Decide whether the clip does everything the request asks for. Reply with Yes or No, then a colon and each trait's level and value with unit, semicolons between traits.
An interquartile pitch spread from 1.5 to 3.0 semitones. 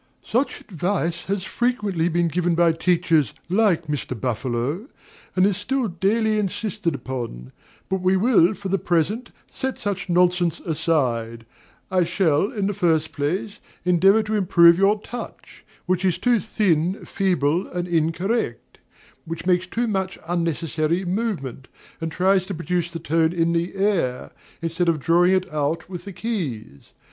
No: average, 3.4 semitones